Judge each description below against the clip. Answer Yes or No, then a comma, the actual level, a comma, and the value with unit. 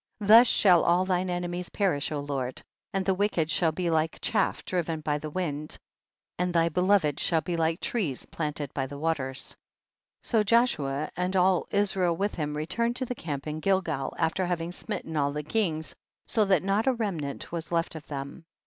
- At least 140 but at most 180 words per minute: No, average, 195 wpm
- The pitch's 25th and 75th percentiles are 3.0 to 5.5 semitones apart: Yes, average, 4.0 semitones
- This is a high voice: No, medium, 170 Hz